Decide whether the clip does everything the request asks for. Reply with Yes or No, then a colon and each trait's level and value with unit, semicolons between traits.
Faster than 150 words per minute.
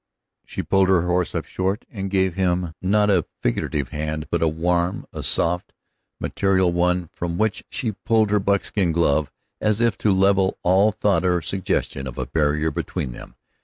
Yes: average, 180 wpm